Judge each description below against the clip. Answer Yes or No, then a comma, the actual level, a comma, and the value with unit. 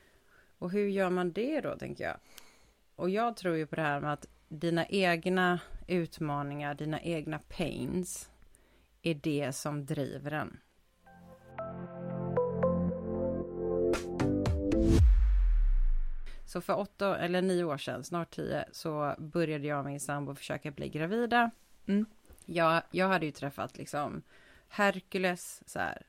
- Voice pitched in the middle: Yes, medium, 160 Hz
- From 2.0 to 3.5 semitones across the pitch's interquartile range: No, average, 4.2 semitones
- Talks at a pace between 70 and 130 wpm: Yes, slow, 125 wpm